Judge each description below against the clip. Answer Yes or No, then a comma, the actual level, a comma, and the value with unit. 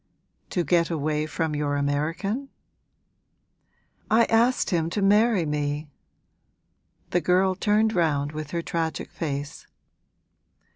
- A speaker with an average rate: No, slow, 110 wpm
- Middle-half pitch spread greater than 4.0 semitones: Yes, average, 4.7 semitones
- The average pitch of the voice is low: No, medium, 165 Hz